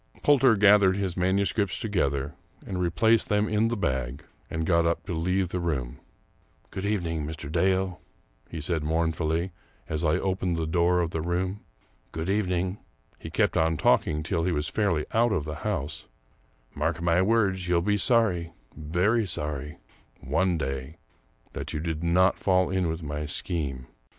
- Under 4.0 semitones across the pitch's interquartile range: Yes, average, 3.3 semitones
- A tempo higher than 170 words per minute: Yes, average, 185 wpm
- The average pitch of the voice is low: Yes, very low, 85 Hz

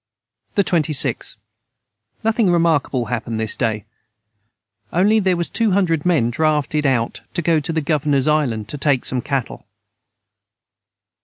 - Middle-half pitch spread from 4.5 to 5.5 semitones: Yes, average, 4.8 semitones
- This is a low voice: No, medium, 150 Hz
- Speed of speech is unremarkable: No, slow, 130 wpm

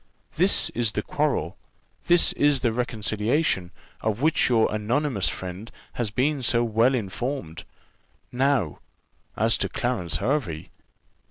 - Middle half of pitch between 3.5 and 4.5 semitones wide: Yes, average, 4.2 semitones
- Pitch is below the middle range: Yes, low, 120 Hz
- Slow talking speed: Yes, slow, 120 wpm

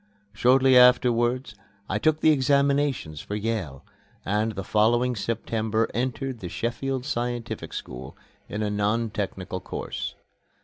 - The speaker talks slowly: Yes, slow, 125 wpm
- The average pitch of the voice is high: No, low, 115 Hz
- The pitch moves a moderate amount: Yes, average, 3.5 semitones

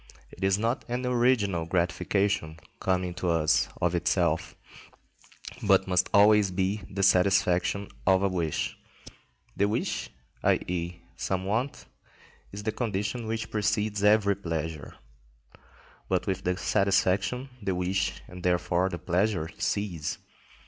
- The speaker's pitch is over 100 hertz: No, very low, 95 Hz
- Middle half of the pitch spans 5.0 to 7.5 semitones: No, average, 2.8 semitones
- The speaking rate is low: Yes, slow, 125 wpm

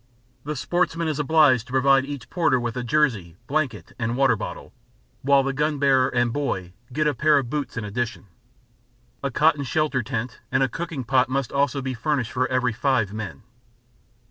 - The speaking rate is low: No, average, 185 wpm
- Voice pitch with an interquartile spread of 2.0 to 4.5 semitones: Yes, average, 3.3 semitones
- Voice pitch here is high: No, low, 130 Hz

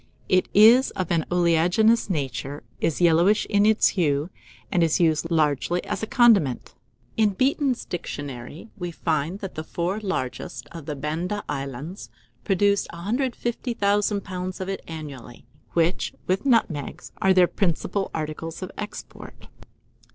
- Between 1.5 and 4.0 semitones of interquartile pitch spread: No, average, 4.5 semitones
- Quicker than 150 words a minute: No, slow, 135 wpm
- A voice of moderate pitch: Yes, medium, 175 Hz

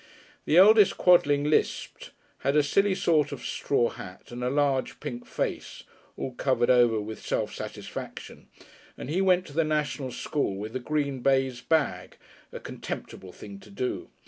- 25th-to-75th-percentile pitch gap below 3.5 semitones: No, average, 4.2 semitones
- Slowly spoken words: No, average, 165 wpm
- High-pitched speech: No, medium, 140 Hz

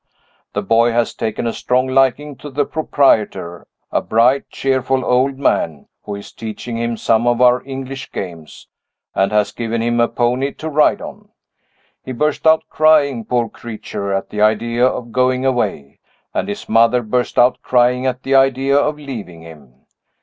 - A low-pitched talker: Yes, low, 125 Hz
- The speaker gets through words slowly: No, average, 170 wpm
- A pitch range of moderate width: Yes, average, 3.1 semitones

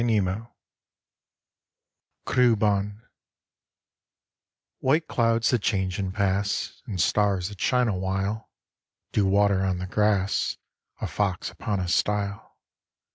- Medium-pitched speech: No, low, 100 Hz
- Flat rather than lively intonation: Yes, narrow, 2.3 semitones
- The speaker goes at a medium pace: No, slow, 110 wpm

